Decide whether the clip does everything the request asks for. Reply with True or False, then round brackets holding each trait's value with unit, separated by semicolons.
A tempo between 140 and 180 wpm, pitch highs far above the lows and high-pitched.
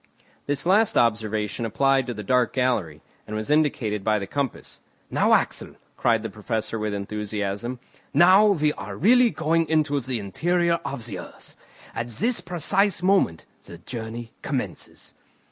False (150 wpm; 7.0 semitones; 120 Hz)